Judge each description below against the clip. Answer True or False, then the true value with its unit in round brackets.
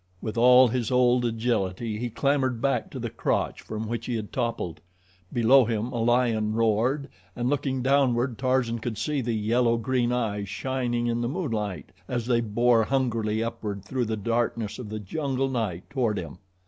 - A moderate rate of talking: True (175 wpm)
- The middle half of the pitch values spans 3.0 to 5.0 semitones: False (2.5 semitones)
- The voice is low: True (120 Hz)